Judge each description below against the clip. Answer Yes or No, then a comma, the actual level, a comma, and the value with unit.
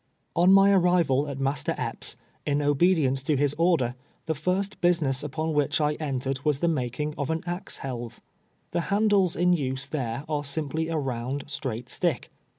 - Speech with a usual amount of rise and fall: Yes, average, 4.2 semitones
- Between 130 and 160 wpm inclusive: No, average, 170 wpm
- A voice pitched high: No, medium, 150 Hz